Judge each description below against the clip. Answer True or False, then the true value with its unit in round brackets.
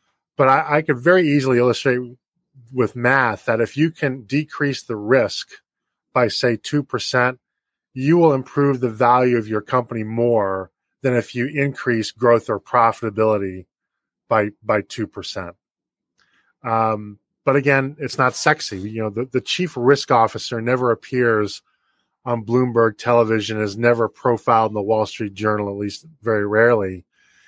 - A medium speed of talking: True (150 wpm)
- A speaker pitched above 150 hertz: False (120 Hz)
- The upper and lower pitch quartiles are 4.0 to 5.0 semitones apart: False (3.3 semitones)